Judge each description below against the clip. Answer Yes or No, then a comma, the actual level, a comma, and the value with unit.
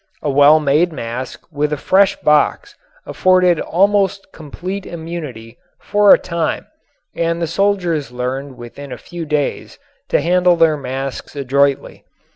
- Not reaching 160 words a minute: Yes, slow, 135 wpm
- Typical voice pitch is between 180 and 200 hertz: No, medium, 155 Hz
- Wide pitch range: No, average, 4.3 semitones